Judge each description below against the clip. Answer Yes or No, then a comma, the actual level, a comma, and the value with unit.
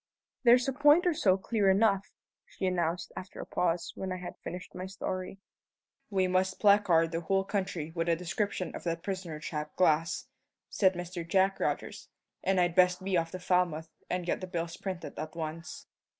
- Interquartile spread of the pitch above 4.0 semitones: No, narrow, 2.4 semitones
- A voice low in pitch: No, medium, 185 Hz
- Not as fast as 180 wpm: No, average, 185 wpm